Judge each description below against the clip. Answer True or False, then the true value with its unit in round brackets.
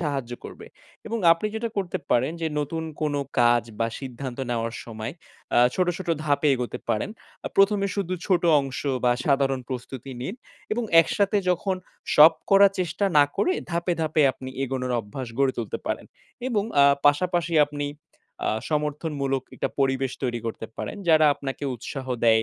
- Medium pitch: True (145 Hz)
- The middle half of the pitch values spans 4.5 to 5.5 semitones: True (5.2 semitones)